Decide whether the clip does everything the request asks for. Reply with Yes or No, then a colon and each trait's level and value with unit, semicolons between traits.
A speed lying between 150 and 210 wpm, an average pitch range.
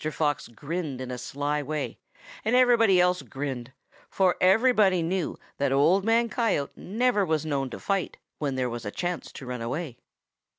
No: average, 170 wpm; wide, 6.2 semitones